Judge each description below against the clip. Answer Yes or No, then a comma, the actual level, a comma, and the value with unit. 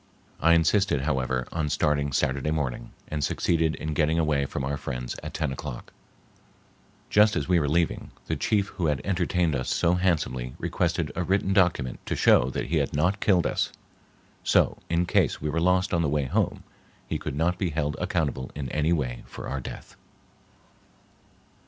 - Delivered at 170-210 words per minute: Yes, average, 180 wpm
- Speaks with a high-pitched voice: No, very low, 75 Hz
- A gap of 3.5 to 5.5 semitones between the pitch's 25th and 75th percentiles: Yes, average, 4.0 semitones